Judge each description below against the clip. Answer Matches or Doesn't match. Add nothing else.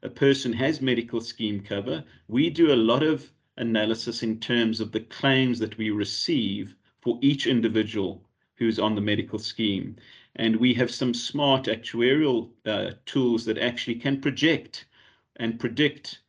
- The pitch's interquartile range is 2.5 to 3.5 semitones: Matches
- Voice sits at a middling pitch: Doesn't match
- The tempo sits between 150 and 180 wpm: Matches